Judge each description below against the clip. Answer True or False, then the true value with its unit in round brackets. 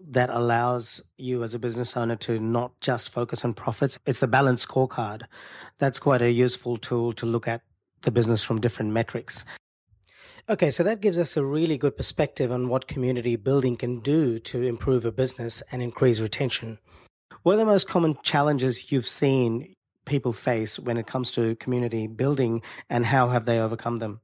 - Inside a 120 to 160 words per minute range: False (185 wpm)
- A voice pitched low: True (125 Hz)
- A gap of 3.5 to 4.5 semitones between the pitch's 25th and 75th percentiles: False (2.7 semitones)